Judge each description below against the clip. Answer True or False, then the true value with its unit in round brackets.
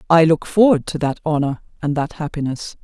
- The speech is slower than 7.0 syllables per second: True (5.5 syllables/s)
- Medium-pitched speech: True (155 Hz)